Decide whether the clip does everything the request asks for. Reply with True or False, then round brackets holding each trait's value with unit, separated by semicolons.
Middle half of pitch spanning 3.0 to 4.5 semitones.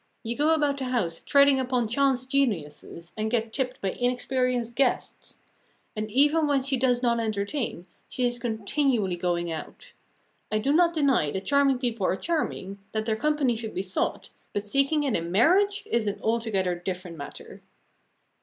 False (5.4 semitones)